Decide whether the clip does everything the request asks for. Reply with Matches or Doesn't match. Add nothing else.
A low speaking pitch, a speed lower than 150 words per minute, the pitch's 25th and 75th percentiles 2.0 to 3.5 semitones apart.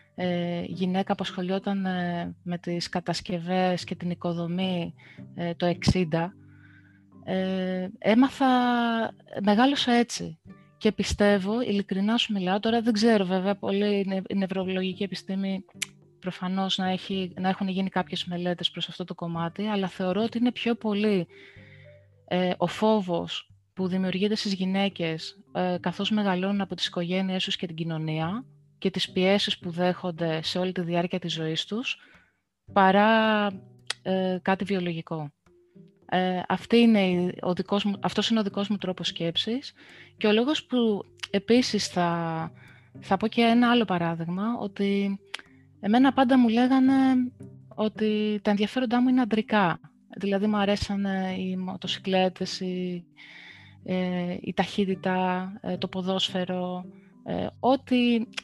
Doesn't match